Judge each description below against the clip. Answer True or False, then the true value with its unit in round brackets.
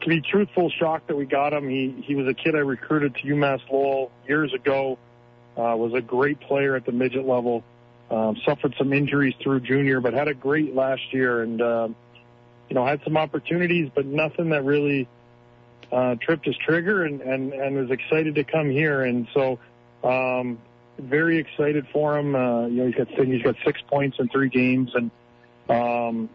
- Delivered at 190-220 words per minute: True (195 wpm)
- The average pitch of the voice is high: False (135 Hz)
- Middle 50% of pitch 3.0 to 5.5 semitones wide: True (3.4 semitones)